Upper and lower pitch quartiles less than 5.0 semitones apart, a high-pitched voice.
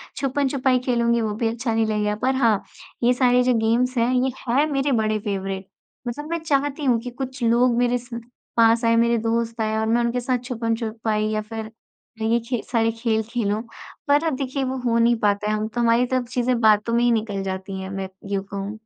Yes: narrow, 2.4 semitones; high, 235 Hz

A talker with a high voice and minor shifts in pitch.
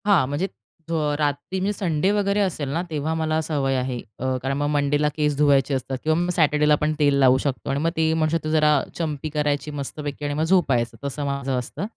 No: medium, 150 Hz; narrow, 2.3 semitones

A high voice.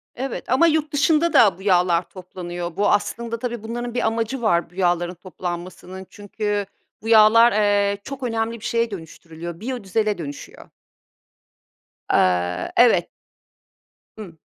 Yes: high, 205 Hz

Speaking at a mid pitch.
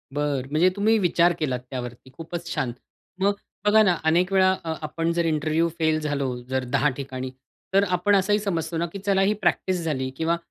Yes: medium, 165 Hz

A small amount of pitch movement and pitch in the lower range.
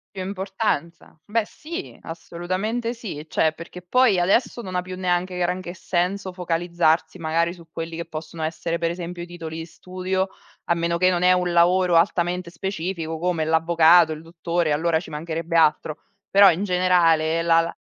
No: narrow, 1.9 semitones; medium, 175 Hz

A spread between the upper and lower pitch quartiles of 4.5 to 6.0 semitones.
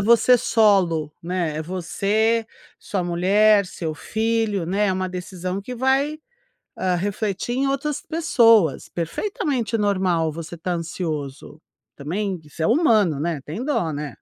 Yes: average, 5.2 semitones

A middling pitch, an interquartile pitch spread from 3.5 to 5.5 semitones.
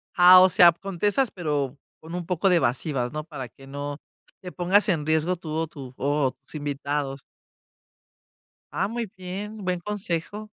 Yes: medium, 165 Hz; average, 4.3 semitones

